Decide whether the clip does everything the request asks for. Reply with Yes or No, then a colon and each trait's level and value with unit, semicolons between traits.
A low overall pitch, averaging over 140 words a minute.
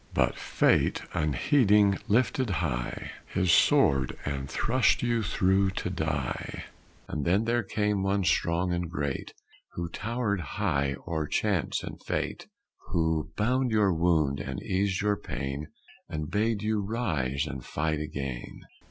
No: very low, 90 Hz; slow, 135 wpm